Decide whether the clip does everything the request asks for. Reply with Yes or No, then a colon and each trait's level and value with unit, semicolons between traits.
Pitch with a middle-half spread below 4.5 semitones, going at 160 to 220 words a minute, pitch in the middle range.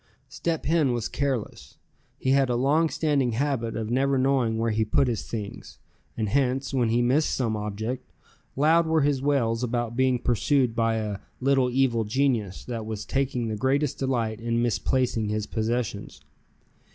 No: average, 3.3 semitones; average, 165 wpm; low, 125 Hz